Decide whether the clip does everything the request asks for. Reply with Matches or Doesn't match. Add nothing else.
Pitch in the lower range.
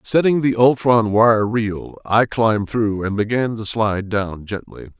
Matches